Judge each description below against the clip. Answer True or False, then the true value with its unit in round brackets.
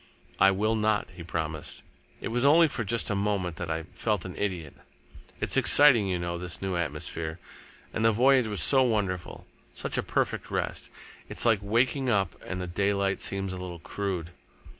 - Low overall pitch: True (100 Hz)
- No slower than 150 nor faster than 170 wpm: False (185 wpm)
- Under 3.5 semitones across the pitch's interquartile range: False (4.2 semitones)